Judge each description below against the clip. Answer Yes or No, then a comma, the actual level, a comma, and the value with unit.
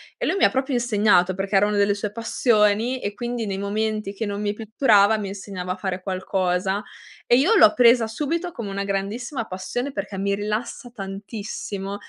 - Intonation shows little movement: No, average, 3.0 semitones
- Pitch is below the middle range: No, high, 205 Hz